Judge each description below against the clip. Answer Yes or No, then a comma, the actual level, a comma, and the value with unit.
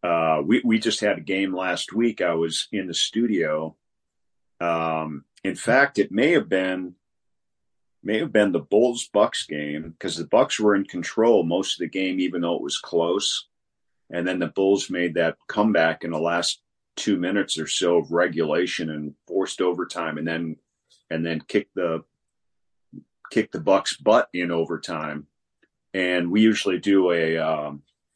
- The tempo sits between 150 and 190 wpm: Yes, average, 170 wpm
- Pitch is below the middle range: Yes, very low, 85 Hz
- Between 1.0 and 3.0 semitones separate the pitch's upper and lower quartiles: Yes, average, 2.7 semitones